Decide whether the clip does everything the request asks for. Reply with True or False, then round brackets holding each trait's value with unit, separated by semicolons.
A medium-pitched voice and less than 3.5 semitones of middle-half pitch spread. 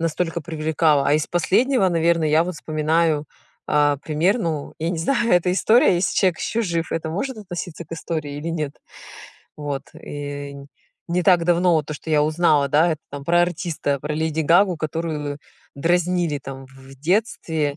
True (160 Hz; 2.9 semitones)